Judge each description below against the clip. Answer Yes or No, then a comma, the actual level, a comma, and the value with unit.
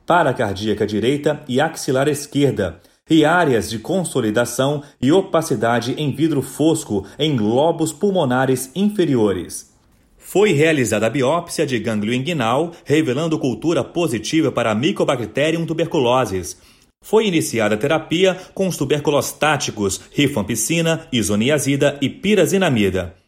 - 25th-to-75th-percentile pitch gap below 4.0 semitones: No, average, 5.3 semitones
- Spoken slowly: Yes, slow, 115 wpm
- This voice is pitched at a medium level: Yes, medium, 145 Hz